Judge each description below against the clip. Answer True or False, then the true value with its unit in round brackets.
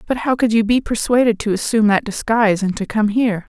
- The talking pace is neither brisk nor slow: False (235 wpm)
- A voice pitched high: True (220 Hz)